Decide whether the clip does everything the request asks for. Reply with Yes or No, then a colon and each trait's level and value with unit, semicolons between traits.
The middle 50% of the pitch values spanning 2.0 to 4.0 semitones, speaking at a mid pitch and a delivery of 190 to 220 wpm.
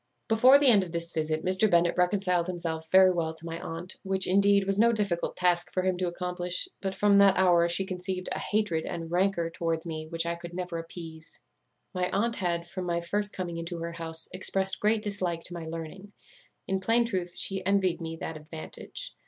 Yes: narrow, 2.4 semitones; medium, 180 Hz; fast, 205 wpm